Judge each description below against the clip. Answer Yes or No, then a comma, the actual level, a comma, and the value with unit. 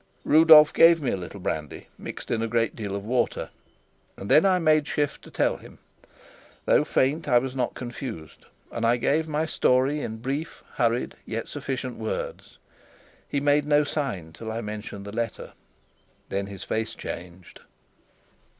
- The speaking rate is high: No, average, 165 wpm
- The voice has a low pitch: Yes, low, 125 Hz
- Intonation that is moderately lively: No, wide, 5.9 semitones